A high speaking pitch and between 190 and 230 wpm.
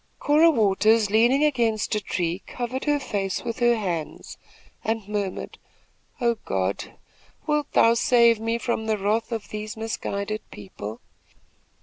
No: high, 220 Hz; slow, 135 wpm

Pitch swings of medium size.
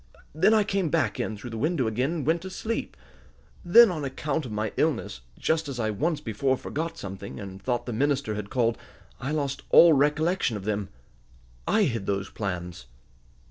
No: wide, 6.9 semitones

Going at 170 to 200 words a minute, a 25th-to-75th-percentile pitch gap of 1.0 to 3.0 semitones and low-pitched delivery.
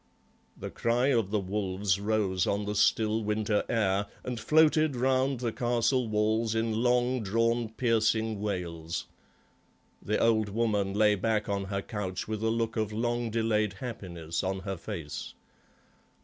No: average, 150 wpm; narrow, 2.6 semitones; low, 110 Hz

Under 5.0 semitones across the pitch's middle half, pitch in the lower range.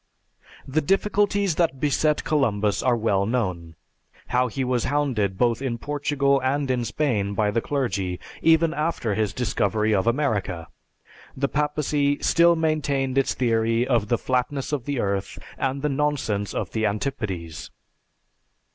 No: wide, 5.4 semitones; low, 130 Hz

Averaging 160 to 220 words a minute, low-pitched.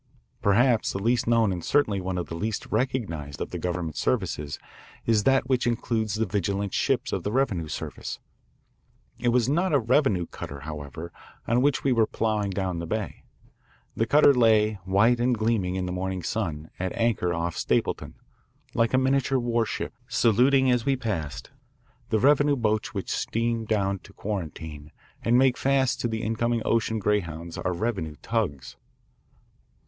Yes: average, 165 wpm; low, 110 Hz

